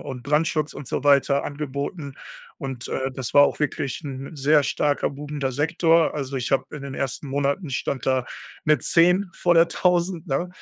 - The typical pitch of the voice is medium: Yes, medium, 145 Hz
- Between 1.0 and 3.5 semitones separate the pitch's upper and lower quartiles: Yes, average, 2.8 semitones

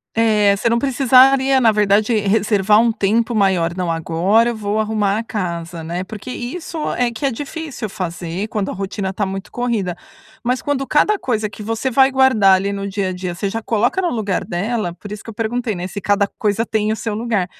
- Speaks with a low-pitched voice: No, high, 215 Hz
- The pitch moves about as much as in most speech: Yes, average, 3.5 semitones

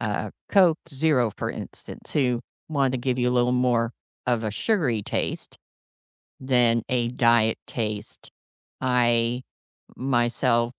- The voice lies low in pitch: Yes, low, 125 Hz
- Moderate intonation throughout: No, narrow, 1.8 semitones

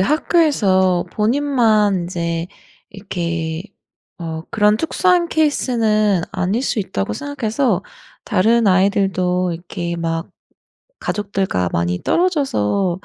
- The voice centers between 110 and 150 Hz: No, high, 195 Hz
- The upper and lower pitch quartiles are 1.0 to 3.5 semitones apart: No, average, 5.1 semitones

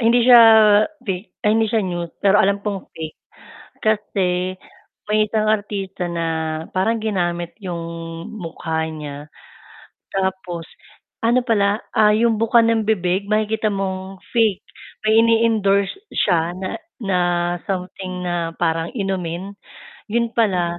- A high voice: Yes, high, 195 Hz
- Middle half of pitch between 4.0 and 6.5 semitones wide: No, average, 3.6 semitones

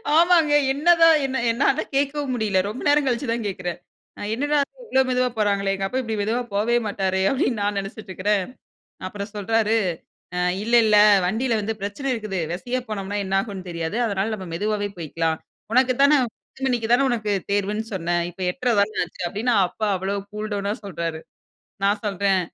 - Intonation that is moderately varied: Yes, average, 4.2 semitones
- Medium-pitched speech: No, high, 210 Hz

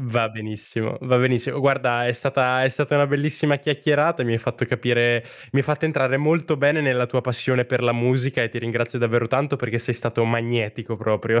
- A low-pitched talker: Yes, low, 125 Hz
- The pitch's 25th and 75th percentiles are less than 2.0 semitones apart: No, average, 2.8 semitones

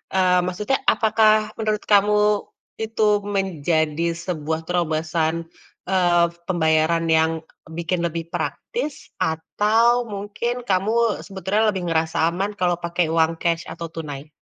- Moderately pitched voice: Yes, medium, 175 Hz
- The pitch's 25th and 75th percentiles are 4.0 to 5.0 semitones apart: Yes, average, 4.4 semitones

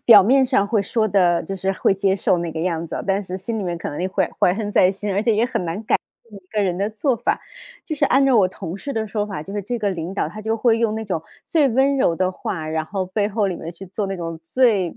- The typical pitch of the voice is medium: No, high, 200 Hz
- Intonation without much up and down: No, average, 3.4 semitones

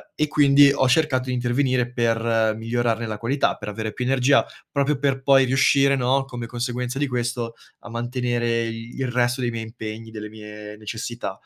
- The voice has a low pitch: Yes, low, 120 Hz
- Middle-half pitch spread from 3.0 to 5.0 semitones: No, narrow, 2.6 semitones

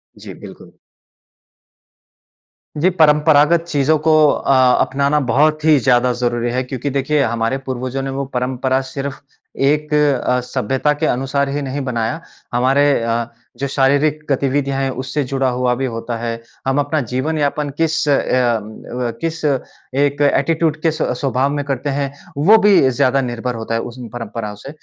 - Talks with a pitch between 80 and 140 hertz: Yes, low, 135 Hz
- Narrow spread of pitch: No, average, 3.0 semitones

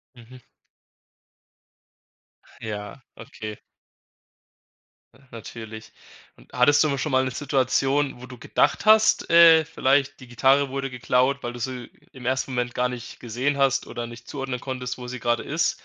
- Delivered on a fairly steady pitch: Yes, narrow, 2.2 semitones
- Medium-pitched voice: No, low, 130 Hz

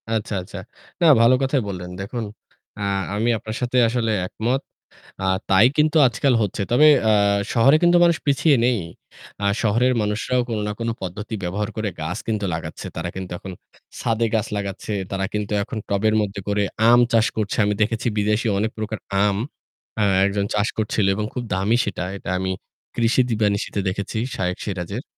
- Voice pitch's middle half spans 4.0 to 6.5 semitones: No, average, 2.9 semitones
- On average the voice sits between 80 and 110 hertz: Yes, low, 105 Hz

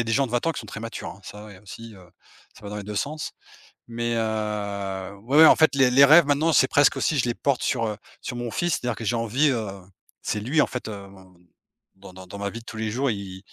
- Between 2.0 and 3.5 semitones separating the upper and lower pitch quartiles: No, average, 4.6 semitones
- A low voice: Yes, low, 115 Hz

